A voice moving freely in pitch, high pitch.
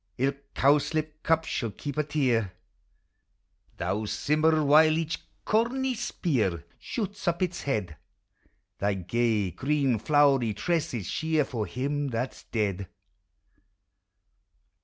No: wide, 6.1 semitones; medium, 140 Hz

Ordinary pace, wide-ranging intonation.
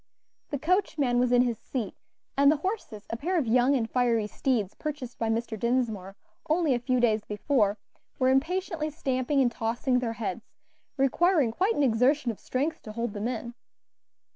No: average, 175 wpm; average, 4.0 semitones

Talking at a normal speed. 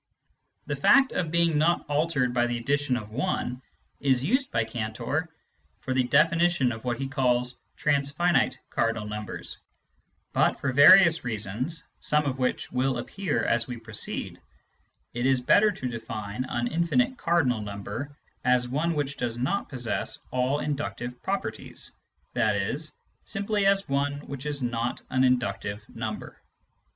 Yes: average, 150 wpm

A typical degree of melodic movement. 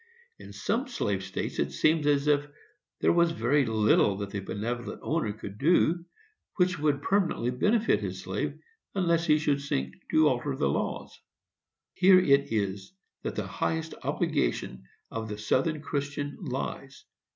No: wide, 7.0 semitones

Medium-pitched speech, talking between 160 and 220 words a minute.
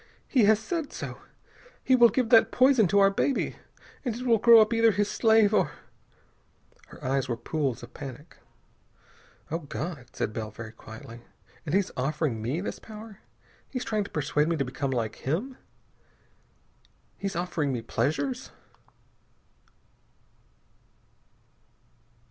No: medium, 175 Hz; average, 145 wpm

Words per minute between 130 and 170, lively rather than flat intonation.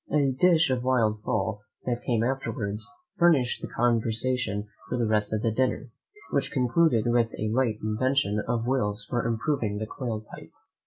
No: average, 160 wpm; average, 3.1 semitones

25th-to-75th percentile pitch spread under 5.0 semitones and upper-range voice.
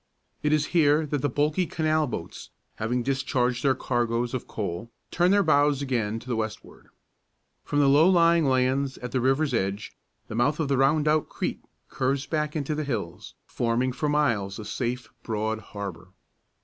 No: average, 4.2 semitones; low, 130 Hz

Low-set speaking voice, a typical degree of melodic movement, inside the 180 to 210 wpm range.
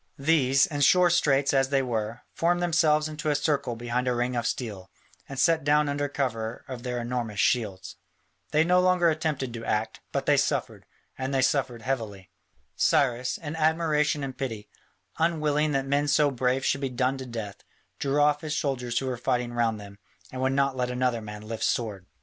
Yes: low, 130 Hz; average, 3.7 semitones; average, 190 wpm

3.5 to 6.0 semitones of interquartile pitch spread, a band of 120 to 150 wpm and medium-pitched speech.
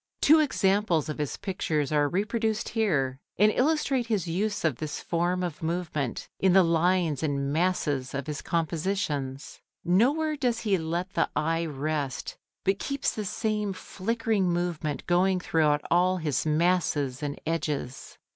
Yes: average, 4.9 semitones; average, 145 wpm; medium, 175 Hz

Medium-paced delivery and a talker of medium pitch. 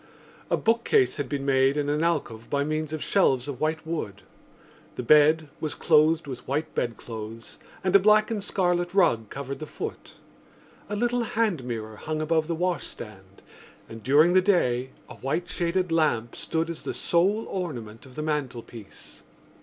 Yes: average, 170 wpm; medium, 155 Hz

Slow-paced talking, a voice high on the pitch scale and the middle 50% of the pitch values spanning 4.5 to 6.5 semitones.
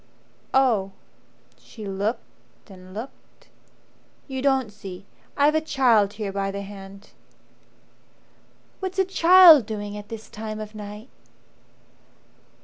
Yes: slow, 115 wpm; high, 215 Hz; average, 5.0 semitones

